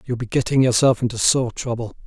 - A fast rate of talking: Yes, fast, 230 wpm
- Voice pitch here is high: No, low, 120 Hz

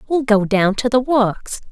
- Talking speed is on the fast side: Yes, fast, 210 wpm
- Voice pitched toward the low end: No, high, 230 Hz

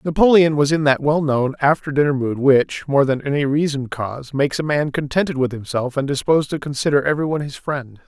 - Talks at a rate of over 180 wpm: Yes, average, 200 wpm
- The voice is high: No, medium, 145 Hz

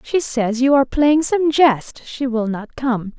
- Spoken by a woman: Yes, female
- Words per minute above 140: Yes, fast, 205 wpm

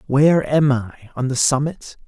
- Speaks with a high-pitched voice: No, medium, 140 Hz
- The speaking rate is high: No, average, 145 wpm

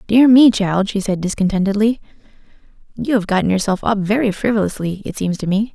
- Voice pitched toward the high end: Yes, high, 205 Hz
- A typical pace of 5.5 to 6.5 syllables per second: Yes, 5.9 syllables/s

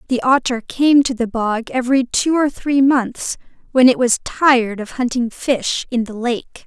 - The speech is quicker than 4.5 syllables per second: No, 4.4 syllables/s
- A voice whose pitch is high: Yes, very high, 250 Hz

